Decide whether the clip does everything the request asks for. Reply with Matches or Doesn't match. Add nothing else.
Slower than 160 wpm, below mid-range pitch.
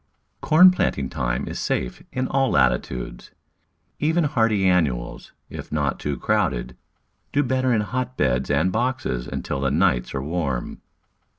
Matches